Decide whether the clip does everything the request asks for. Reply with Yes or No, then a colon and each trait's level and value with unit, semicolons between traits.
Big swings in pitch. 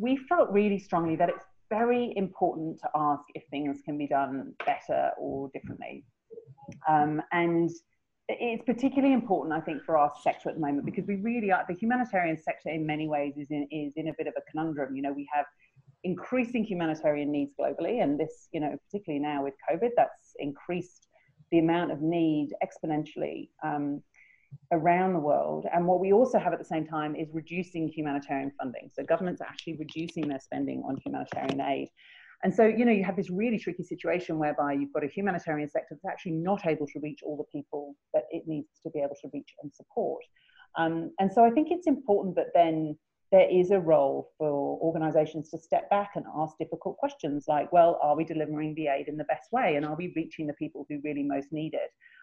No: average, 4.1 semitones